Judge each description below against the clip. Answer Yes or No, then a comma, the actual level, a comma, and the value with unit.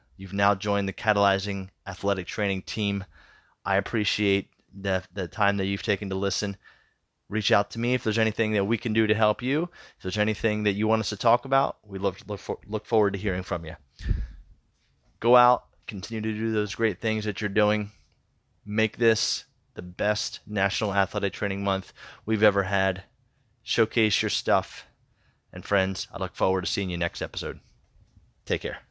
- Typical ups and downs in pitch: No, narrow, 2.1 semitones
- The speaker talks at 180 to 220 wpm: Yes, average, 185 wpm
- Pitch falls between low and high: No, low, 105 Hz